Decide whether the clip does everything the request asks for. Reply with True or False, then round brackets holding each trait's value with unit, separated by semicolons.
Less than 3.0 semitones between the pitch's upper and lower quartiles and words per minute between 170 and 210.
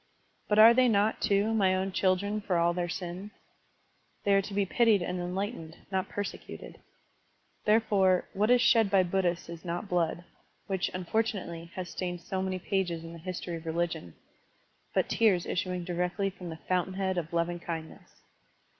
True (2.6 semitones; 180 wpm)